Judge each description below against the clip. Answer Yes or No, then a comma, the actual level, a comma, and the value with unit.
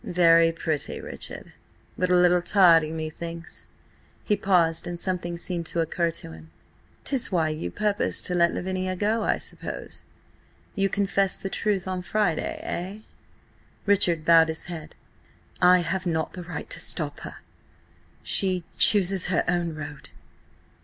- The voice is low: No, medium, 175 Hz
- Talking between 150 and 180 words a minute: No, average, 140 wpm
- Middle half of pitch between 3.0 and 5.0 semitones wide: No, narrow, 2.4 semitones